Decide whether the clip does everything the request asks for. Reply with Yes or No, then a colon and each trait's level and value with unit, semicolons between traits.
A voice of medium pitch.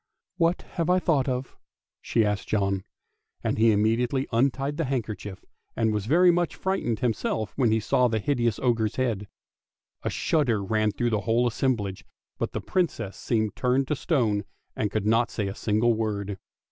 No: low, 115 Hz